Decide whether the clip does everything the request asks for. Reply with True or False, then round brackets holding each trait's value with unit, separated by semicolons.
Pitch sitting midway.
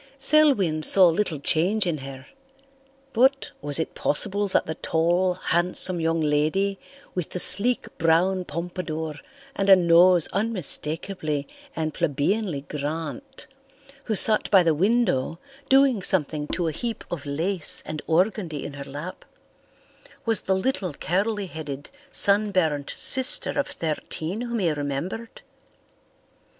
True (175 Hz)